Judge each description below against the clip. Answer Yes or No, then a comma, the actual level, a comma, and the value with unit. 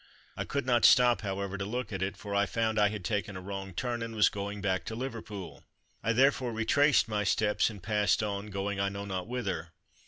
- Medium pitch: No, low, 105 Hz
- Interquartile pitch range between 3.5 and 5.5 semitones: No, narrow, 2.6 semitones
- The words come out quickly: Yes, fast, 220 wpm